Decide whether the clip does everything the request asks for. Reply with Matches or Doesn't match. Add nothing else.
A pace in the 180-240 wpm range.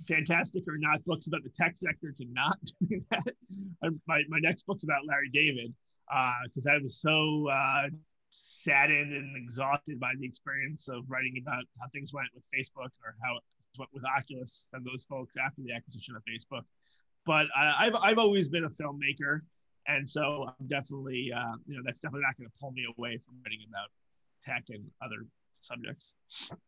Matches